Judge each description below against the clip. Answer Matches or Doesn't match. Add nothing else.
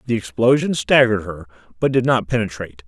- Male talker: Matches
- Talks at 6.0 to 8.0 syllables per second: Matches